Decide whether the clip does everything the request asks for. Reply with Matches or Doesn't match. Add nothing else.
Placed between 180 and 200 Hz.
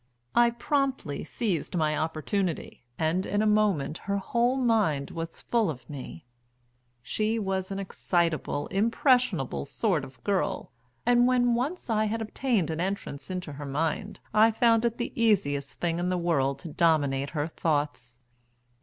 Matches